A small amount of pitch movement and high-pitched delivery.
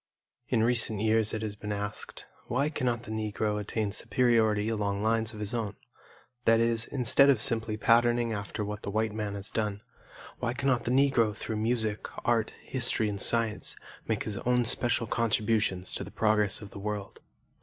No: narrow, 2.1 semitones; low, 110 Hz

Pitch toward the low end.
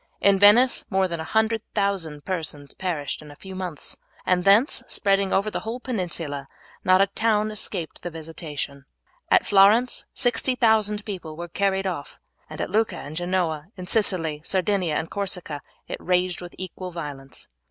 No: medium, 185 Hz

